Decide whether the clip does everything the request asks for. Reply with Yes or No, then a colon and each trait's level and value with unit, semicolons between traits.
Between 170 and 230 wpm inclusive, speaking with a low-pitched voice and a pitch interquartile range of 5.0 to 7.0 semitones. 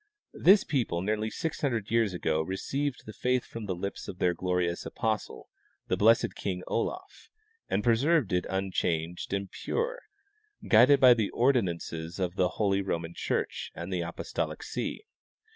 No: average, 150 wpm; low, 100 Hz; wide, 5.4 semitones